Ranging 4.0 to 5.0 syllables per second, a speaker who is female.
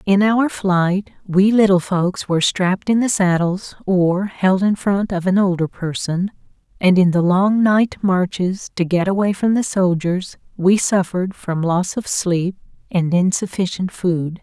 Yes: 4.1 syllables/s; female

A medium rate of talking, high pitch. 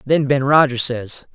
No: average, 180 wpm; low, 135 Hz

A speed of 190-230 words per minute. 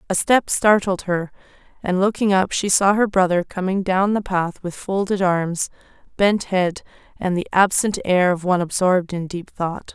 No: average, 180 wpm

